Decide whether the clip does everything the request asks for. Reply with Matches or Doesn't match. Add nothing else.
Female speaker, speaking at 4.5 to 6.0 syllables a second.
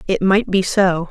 Doesn't match